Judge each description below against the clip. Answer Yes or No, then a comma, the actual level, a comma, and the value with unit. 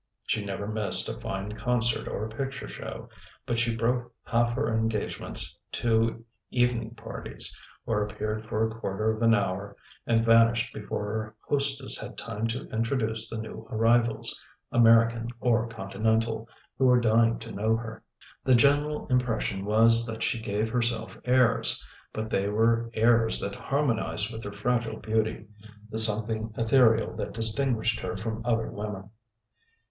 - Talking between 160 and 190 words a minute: No, average, 150 wpm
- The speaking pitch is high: No, low, 115 Hz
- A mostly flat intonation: Yes, narrow, 1.4 semitones